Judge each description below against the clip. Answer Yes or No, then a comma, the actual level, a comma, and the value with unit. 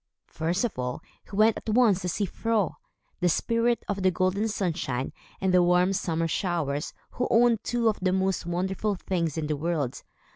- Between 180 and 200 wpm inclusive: Yes, average, 185 wpm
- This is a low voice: No, medium, 185 Hz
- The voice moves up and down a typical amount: Yes, average, 4.2 semitones